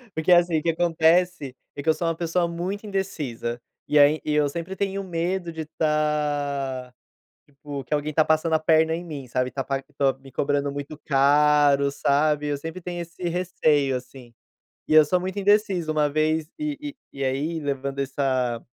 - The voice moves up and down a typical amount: Yes, average, 3.3 semitones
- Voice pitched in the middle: Yes, medium, 155 Hz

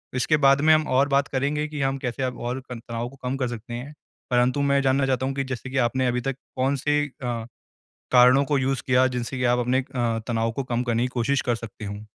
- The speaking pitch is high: No, low, 130 Hz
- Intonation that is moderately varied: No, narrow, 2.1 semitones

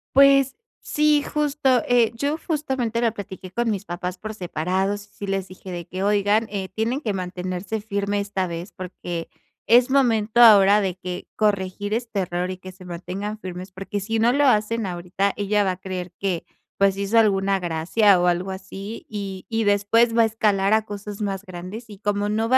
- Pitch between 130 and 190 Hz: No, high, 200 Hz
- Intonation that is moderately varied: Yes, average, 3.2 semitones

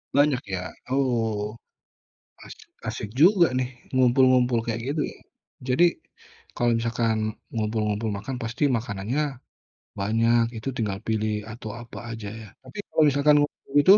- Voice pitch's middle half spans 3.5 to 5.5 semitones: No, average, 3.1 semitones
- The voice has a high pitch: No, low, 115 Hz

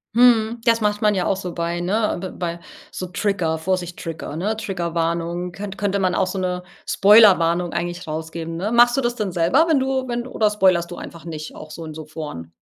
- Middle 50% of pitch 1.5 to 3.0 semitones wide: No, average, 4.0 semitones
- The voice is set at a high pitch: No, medium, 180 Hz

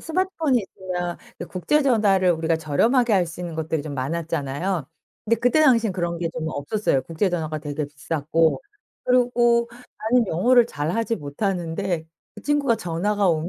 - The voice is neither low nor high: Yes, medium, 180 Hz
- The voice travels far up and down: Yes, wide, 6.3 semitones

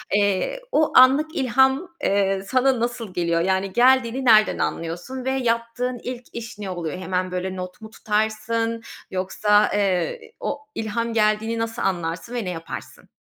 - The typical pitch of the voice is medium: No, high, 220 Hz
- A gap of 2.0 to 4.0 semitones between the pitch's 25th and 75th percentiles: No, average, 4.5 semitones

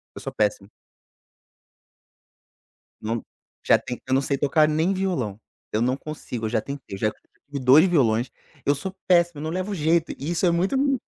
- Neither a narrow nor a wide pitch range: No, wide, 5.8 semitones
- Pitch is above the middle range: No, medium, 145 Hz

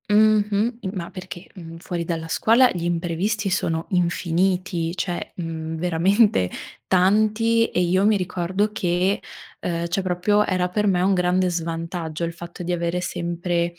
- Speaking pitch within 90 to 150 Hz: No, medium, 180 Hz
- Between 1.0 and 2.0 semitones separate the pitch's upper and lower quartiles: No, average, 2.7 semitones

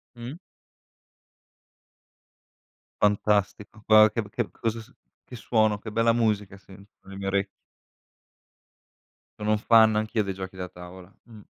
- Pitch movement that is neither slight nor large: No, narrow, 2.2 semitones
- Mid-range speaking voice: No, low, 105 Hz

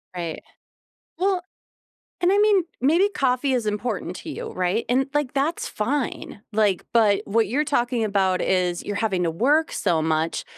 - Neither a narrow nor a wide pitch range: No, wide, 7.2 semitones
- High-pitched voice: Yes, high, 225 Hz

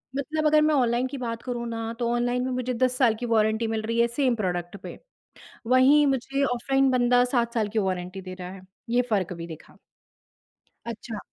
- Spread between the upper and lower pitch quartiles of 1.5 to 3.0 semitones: Yes, average, 2.7 semitones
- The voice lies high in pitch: Yes, high, 235 Hz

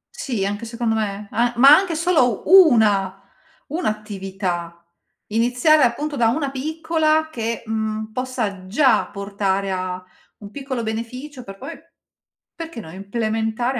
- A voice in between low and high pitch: No, high, 230 Hz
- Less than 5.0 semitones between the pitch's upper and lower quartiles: No, wide, 5.4 semitones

